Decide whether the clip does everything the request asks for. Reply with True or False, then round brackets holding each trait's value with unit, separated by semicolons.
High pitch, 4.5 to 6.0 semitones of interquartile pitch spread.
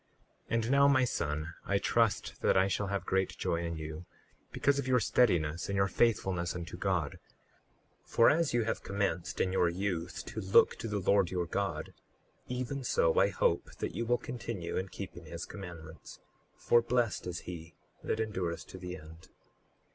False (95 Hz; 5.3 semitones)